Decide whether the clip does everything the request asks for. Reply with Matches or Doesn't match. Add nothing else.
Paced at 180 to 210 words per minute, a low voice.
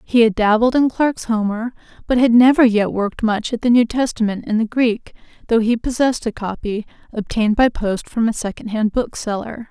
Doesn't match